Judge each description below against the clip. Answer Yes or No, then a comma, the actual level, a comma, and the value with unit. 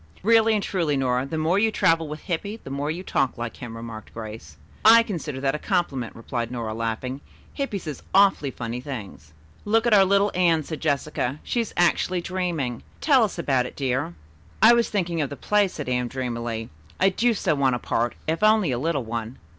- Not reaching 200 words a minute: No, fast, 205 wpm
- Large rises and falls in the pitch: Yes, wide, 7.7 semitones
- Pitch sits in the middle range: Yes, medium, 150 Hz